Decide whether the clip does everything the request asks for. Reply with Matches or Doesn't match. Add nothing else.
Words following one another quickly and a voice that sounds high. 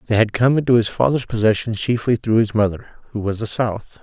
Doesn't match